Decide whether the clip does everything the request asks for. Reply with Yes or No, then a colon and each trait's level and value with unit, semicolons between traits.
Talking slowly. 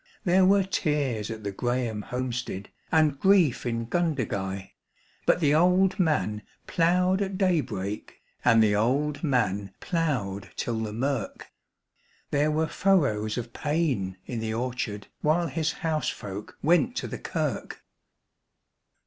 Yes: slow, 130 wpm